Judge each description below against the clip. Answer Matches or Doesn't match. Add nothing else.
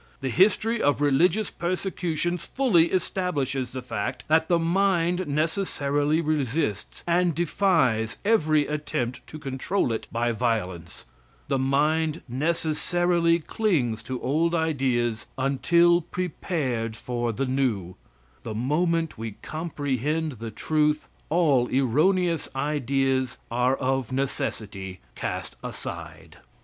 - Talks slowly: Matches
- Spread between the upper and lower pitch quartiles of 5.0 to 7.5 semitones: Matches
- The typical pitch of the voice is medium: Matches